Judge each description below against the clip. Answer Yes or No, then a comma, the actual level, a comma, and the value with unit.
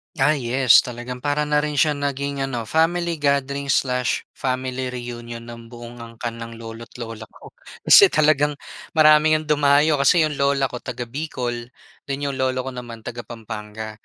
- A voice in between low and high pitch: No, low, 130 Hz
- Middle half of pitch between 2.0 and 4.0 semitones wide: Yes, average, 3.6 semitones